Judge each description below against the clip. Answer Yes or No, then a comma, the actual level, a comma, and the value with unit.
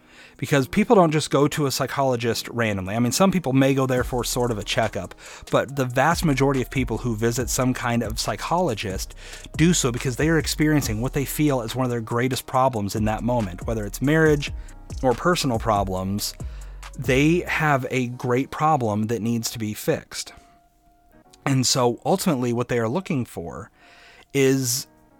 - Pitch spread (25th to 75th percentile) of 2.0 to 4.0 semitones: Yes, average, 3.4 semitones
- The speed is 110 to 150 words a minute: No, average, 180 wpm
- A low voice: Yes, low, 130 Hz